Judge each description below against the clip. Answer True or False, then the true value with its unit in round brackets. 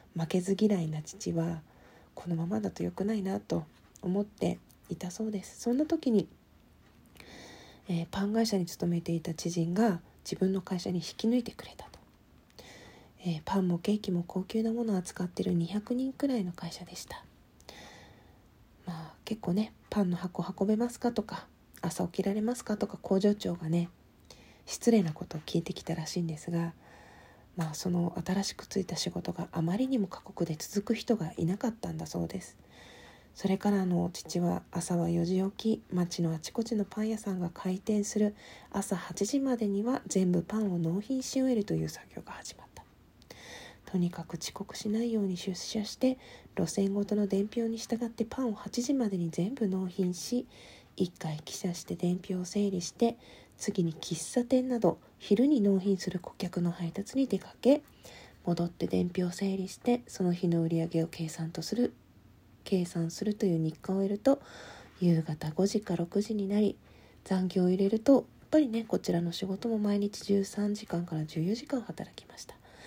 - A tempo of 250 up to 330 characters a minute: True (315 characters per minute)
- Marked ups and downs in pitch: False (3.9 semitones)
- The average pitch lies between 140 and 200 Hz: True (190 Hz)